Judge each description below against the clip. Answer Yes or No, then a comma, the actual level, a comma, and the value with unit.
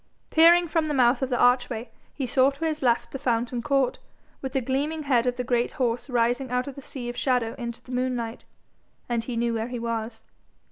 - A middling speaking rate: No, fast, 215 wpm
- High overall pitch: Yes, very high, 250 Hz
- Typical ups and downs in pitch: No, narrow, 2.3 semitones